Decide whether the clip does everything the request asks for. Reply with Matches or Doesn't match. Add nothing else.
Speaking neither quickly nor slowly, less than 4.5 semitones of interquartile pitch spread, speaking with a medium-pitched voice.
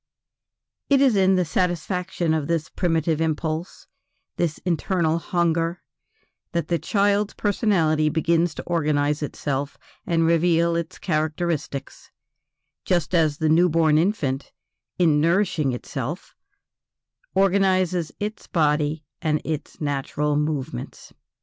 Doesn't match